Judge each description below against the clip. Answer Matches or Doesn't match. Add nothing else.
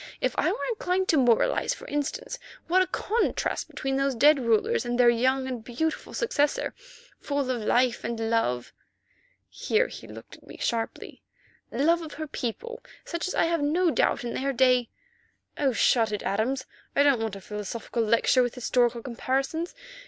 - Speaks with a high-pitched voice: Matches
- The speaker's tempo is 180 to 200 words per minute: Doesn't match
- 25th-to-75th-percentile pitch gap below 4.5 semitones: Doesn't match